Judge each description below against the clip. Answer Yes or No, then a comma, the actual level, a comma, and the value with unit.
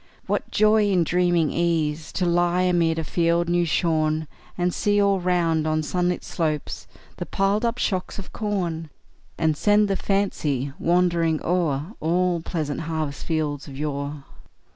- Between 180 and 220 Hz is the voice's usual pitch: No, medium, 170 Hz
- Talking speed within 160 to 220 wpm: No, average, 150 wpm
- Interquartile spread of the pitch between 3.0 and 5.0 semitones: No, narrow, 2.6 semitones